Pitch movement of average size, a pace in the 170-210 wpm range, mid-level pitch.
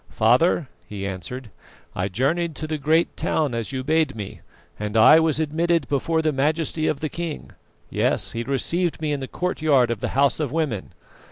Yes: average, 4.6 semitones; average, 185 wpm; medium, 145 Hz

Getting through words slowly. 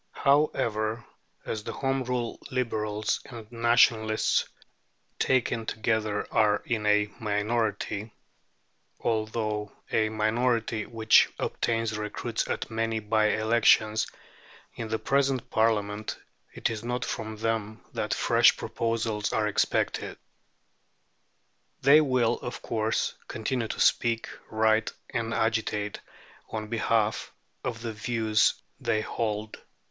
Yes: slow, 110 wpm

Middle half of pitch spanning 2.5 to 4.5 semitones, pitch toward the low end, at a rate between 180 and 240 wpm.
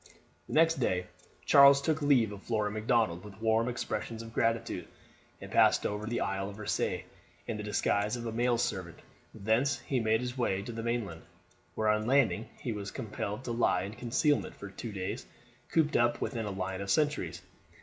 Yes: average, 3.0 semitones; low, 110 Hz; average, 190 wpm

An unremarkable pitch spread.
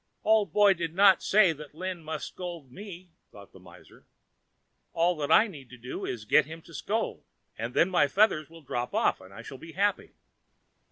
No: wide, 5.8 semitones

